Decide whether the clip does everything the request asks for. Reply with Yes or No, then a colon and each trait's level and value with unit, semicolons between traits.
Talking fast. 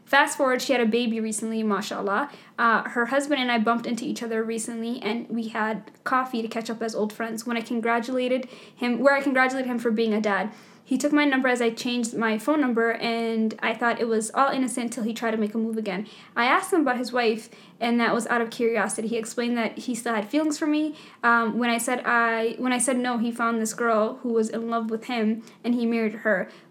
Yes: fast, 245 wpm